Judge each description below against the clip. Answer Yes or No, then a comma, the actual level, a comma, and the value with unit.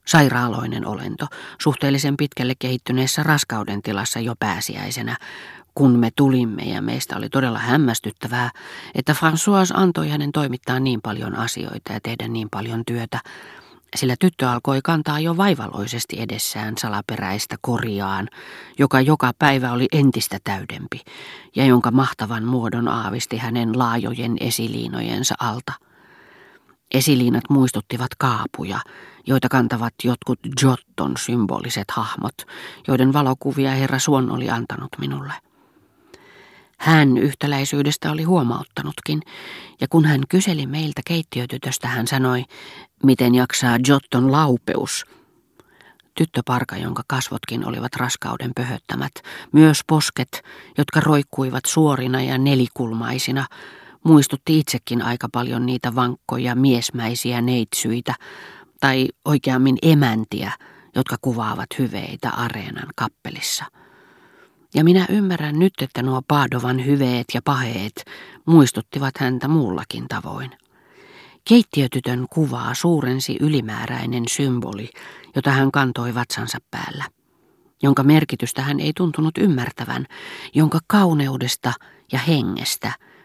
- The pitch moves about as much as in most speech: Yes, average, 3.2 semitones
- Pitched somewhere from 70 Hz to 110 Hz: No, low, 130 Hz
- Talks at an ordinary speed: Yes, average, 105 wpm